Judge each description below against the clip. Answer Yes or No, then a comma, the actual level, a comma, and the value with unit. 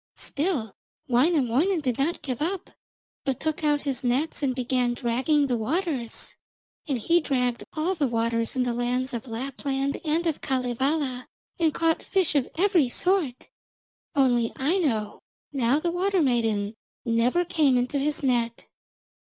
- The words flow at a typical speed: Yes, average, 145 wpm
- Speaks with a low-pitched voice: No, very high, 270 Hz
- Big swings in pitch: No, average, 4.5 semitones